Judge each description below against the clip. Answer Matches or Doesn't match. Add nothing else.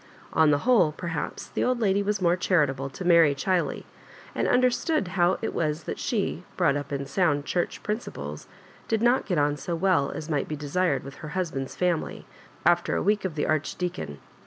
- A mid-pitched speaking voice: Matches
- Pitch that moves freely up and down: Doesn't match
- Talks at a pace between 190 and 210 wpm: Matches